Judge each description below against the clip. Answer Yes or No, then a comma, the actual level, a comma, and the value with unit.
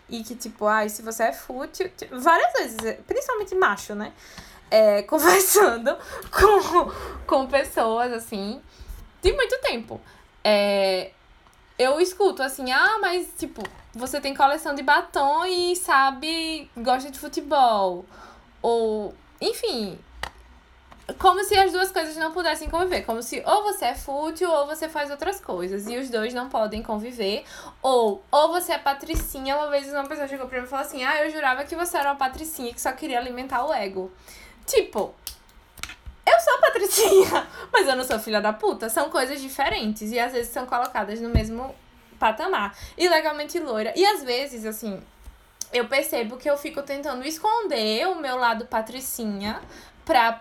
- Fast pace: No, average, 160 wpm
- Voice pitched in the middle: No, very high, 275 Hz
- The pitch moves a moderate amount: No, wide, 6.4 semitones